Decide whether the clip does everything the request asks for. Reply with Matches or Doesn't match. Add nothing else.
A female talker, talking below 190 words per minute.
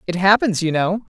Doesn't match